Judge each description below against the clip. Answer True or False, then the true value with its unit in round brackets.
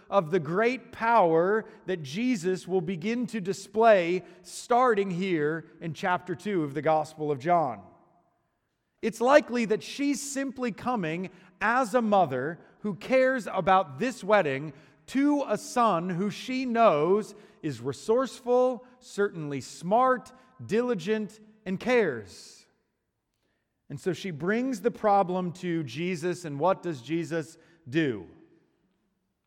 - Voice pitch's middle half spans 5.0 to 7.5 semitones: True (5.6 semitones)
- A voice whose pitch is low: False (195 Hz)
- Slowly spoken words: True (120 wpm)